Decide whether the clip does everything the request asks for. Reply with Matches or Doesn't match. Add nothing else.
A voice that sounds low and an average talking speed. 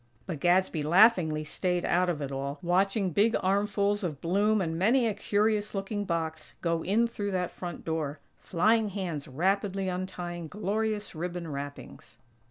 Doesn't match